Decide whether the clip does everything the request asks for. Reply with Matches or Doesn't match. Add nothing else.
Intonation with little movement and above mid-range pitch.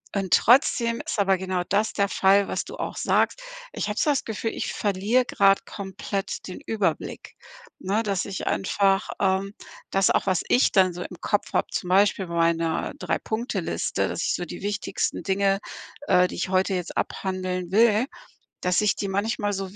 Matches